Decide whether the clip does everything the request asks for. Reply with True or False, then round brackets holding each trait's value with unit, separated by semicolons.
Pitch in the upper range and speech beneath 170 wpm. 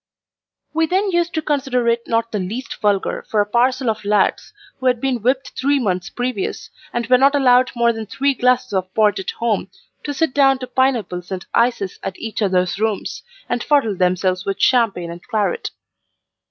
False (235 Hz; 190 wpm)